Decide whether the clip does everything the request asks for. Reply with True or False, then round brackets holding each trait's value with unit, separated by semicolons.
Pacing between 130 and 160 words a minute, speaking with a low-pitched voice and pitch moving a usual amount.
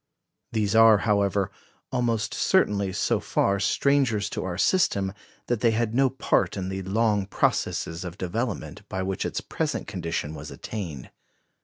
True (150 wpm; 100 Hz; 3.4 semitones)